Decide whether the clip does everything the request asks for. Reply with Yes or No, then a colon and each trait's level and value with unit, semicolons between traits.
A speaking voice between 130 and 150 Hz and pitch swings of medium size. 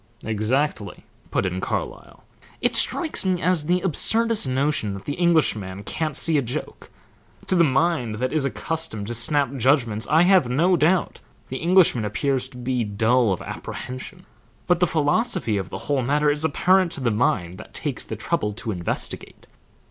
No: medium, 140 Hz; wide, 6.8 semitones